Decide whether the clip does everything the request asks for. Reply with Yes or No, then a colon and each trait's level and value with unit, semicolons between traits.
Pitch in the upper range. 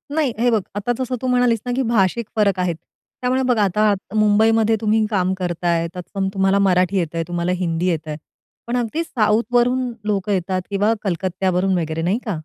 Yes: high, 200 Hz